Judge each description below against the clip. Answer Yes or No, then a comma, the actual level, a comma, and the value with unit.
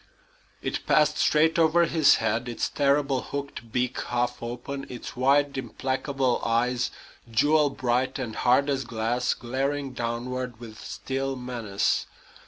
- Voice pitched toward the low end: Yes, low, 130 Hz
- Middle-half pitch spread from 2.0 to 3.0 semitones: Yes, narrow, 2.6 semitones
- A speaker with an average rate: No, slow, 130 wpm